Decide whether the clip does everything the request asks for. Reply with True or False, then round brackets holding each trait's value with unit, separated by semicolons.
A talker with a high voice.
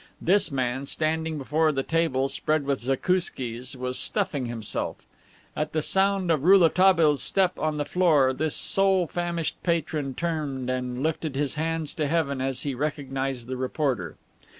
False (150 Hz)